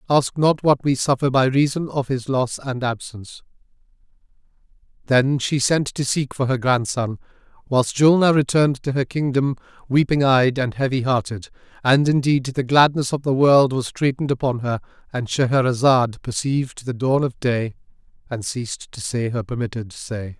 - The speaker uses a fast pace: No, average, 160 wpm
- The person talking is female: No, male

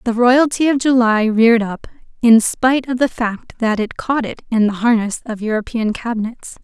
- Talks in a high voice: Yes, high, 230 Hz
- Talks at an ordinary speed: Yes, average, 190 wpm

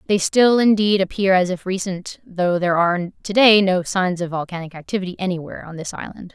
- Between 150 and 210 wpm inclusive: Yes, average, 200 wpm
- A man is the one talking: No, female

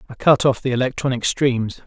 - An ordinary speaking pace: Yes, average, 195 wpm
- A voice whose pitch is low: Yes, low, 130 Hz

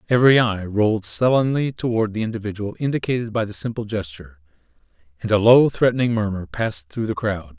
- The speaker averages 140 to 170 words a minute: Yes, average, 165 wpm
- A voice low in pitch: Yes, low, 105 Hz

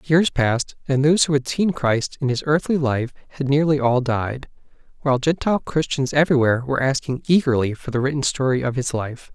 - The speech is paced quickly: No, average, 195 wpm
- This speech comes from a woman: No, male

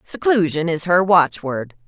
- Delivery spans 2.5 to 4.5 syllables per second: Yes, 4.1 syllables/s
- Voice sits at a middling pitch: Yes, medium, 170 Hz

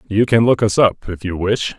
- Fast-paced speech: Yes, fast, 270 wpm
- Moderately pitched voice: No, low, 105 Hz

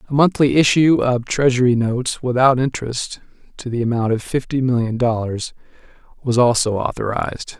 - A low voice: Yes, low, 125 Hz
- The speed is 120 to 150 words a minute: Yes, average, 140 wpm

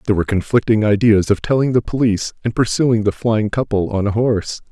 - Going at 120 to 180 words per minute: No, fast, 205 wpm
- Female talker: No, male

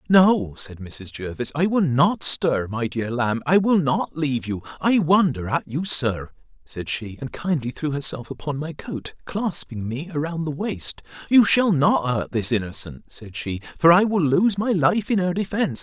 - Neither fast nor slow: Yes, average, 195 wpm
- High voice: No, medium, 150 Hz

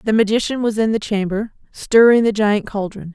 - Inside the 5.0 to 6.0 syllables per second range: Yes, 5.3 syllables/s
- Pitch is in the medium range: No, high, 215 Hz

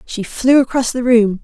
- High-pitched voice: Yes, high, 240 Hz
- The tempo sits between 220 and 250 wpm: No, fast, 210 wpm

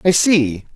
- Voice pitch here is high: No, medium, 150 Hz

